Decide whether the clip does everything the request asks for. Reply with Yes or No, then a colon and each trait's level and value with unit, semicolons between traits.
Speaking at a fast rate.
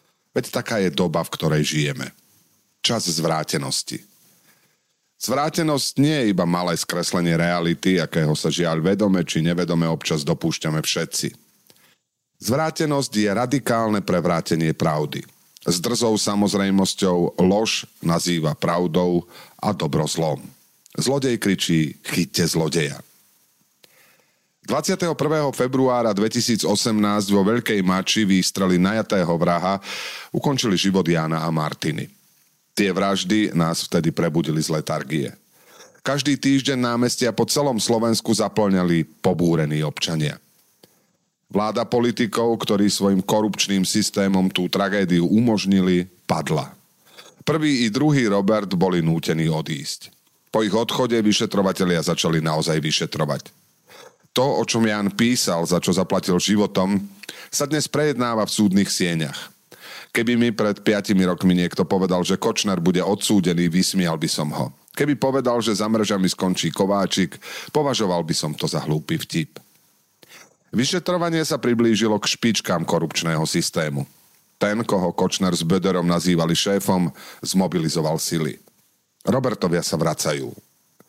No: average, 120 wpm